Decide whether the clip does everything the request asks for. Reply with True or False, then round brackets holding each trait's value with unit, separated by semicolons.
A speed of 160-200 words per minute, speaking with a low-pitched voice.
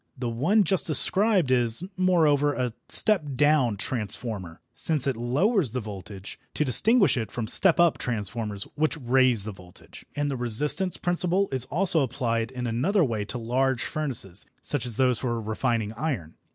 True (165 wpm; 125 Hz)